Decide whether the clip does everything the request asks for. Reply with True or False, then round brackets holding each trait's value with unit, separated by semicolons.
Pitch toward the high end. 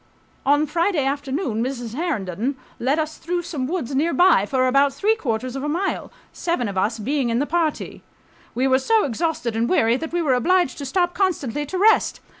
True (285 Hz)